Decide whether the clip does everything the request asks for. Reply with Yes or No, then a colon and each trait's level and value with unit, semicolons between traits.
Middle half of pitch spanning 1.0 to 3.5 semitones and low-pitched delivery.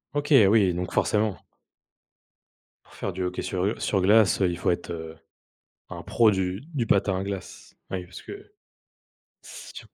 Yes: average, 2.8 semitones; very low, 95 Hz